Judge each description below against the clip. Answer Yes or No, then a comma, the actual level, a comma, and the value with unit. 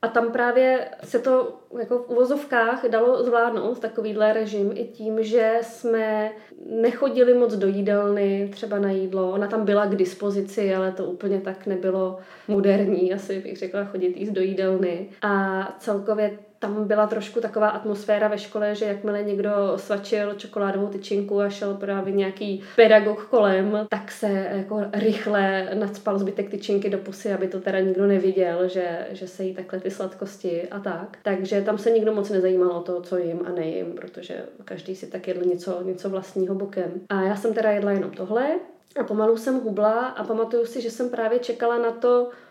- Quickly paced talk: Yes, fast, 180 wpm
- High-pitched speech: Yes, high, 205 Hz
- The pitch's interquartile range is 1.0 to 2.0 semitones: No, narrow, 2.5 semitones